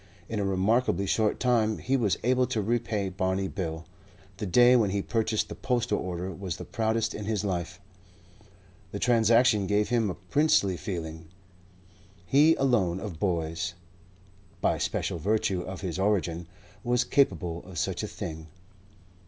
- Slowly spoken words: No, average, 155 wpm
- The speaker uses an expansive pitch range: No, average, 4.2 semitones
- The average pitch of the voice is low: Yes, low, 100 Hz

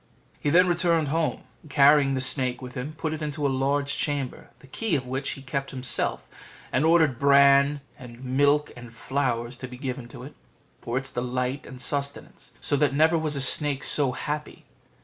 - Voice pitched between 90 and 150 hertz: Yes, medium, 140 Hz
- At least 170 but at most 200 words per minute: Yes, average, 185 wpm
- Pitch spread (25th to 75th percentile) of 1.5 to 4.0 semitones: Yes, narrow, 2.5 semitones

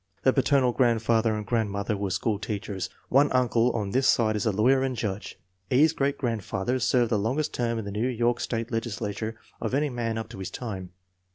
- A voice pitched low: Yes, low, 115 Hz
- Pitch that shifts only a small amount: No, average, 3.0 semitones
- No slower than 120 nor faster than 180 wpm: No, fast, 205 wpm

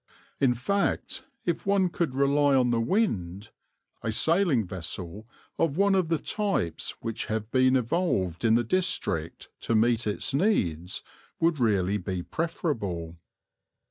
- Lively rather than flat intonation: Yes, wide, 9.0 semitones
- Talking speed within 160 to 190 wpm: No, average, 140 wpm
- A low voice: Yes, low, 120 Hz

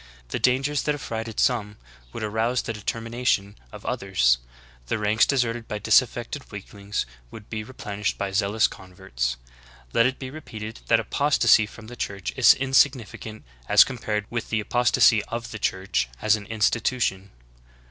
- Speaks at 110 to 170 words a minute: Yes, average, 160 wpm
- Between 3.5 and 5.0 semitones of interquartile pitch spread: No, average, 3.0 semitones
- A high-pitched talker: No, low, 110 Hz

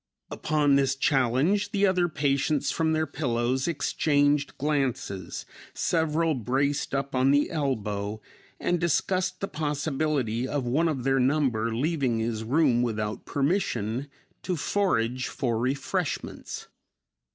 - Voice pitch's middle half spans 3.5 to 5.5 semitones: Yes, average, 4.2 semitones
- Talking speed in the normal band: No, slow, 120 wpm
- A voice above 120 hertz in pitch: Yes, medium, 140 Hz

